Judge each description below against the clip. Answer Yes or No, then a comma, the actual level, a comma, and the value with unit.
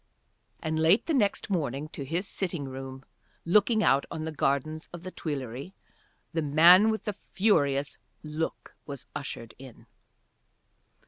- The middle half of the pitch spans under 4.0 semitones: No, average, 5.0 semitones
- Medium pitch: Yes, medium, 155 Hz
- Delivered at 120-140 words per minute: Yes, slow, 135 wpm